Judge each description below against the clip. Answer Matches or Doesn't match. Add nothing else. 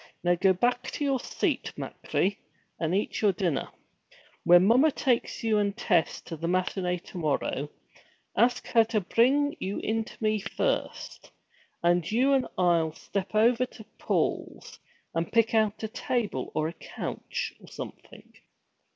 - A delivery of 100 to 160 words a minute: Matches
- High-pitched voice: Matches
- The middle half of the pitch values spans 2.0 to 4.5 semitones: Doesn't match